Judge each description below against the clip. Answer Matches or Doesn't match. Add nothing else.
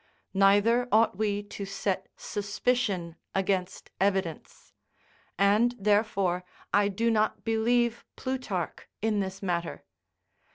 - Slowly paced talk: Matches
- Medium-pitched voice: Doesn't match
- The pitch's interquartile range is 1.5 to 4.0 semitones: Matches